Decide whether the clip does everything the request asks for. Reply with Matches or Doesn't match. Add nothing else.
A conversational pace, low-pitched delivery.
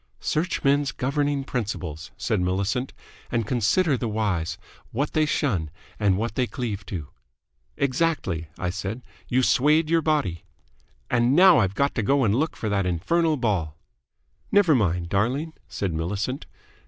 Matches